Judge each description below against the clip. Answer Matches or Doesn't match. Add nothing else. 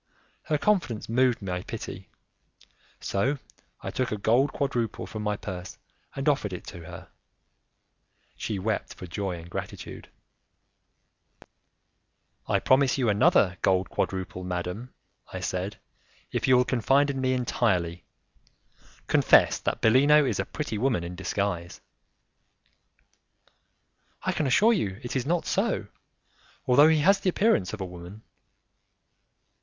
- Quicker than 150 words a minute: Doesn't match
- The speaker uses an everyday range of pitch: Doesn't match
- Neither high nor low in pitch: Doesn't match